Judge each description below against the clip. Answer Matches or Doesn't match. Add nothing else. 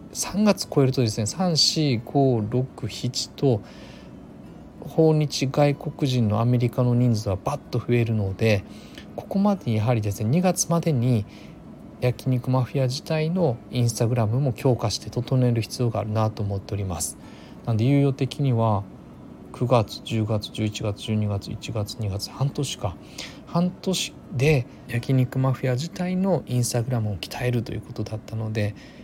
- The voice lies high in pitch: Doesn't match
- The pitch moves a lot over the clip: Doesn't match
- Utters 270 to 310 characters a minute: Matches